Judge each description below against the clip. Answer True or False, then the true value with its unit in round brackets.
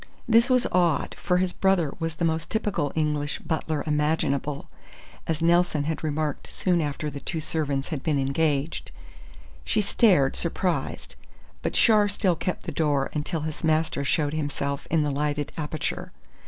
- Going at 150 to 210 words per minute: True (155 wpm)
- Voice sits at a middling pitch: True (155 Hz)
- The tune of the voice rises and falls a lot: False (2.9 semitones)